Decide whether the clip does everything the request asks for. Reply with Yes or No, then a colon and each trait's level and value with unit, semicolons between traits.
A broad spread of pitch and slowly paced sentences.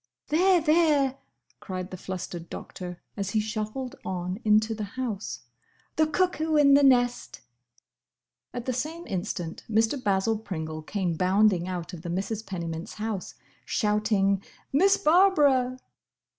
Yes: wide, 6.6 semitones; slow, 130 wpm